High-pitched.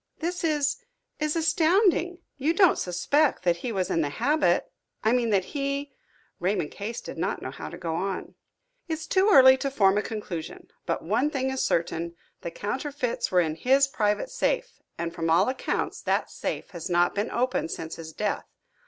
Yes: high, 245 Hz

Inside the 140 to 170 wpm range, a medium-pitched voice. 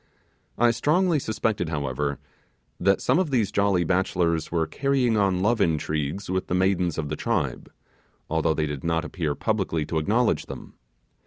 No: average, 160 wpm; very low, 90 Hz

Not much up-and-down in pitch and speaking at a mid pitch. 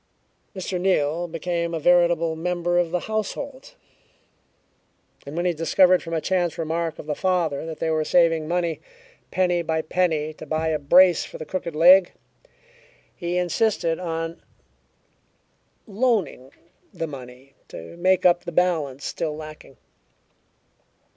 Yes: narrow, 2.2 semitones; medium, 170 Hz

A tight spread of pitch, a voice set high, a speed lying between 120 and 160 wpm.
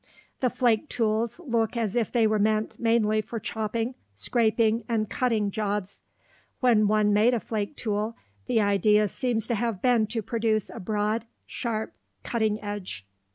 Yes: narrow, 1.8 semitones; high, 220 Hz; average, 155 wpm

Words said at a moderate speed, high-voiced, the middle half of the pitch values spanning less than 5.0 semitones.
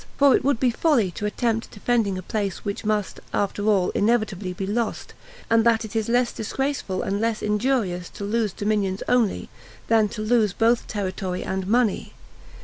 Yes: average, 175 wpm; high, 215 Hz; average, 2.7 semitones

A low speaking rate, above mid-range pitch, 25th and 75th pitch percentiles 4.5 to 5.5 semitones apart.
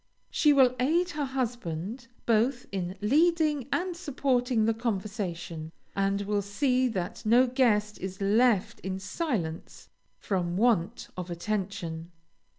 Yes: slow, 125 wpm; high, 215 Hz; average, 5.1 semitones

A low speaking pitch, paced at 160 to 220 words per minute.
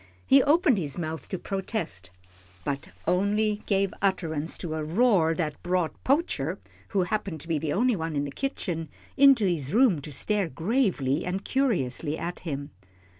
No: medium, 180 Hz; average, 170 wpm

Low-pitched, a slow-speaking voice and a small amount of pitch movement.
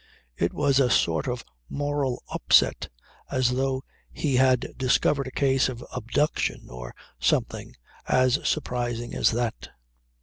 Yes: low, 130 Hz; slow, 130 wpm; narrow, 2.0 semitones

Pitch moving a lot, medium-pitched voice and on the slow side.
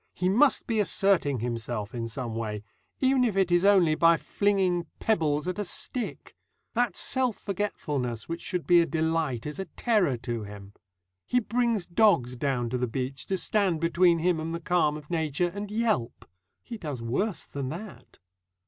No: wide, 7.3 semitones; medium, 170 Hz; average, 175 wpm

